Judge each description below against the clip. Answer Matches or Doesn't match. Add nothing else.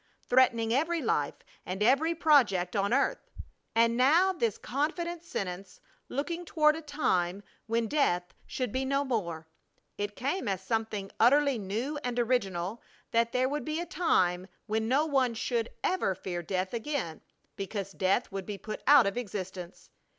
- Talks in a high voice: Matches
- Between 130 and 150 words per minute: Doesn't match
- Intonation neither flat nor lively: Doesn't match